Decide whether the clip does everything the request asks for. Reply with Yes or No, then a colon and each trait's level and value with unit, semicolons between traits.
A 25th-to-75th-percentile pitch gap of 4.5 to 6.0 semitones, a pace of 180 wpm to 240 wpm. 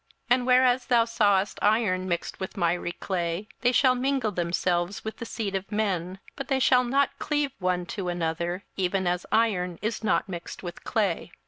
Yes: average, 5.2 semitones; average, 185 wpm